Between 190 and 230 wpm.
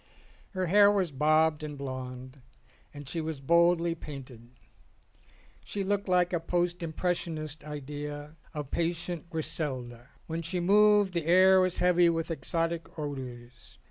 No: slow, 135 wpm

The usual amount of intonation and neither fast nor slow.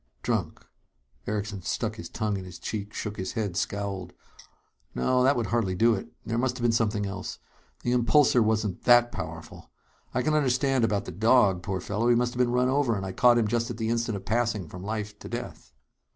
No: average, 3.6 semitones; fast, 215 wpm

